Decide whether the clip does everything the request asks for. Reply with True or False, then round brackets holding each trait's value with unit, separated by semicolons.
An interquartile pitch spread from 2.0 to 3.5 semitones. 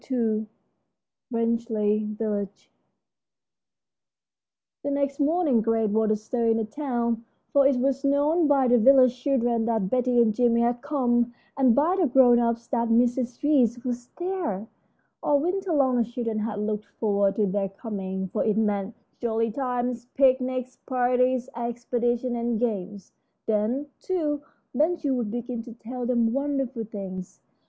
True (3.0 semitones)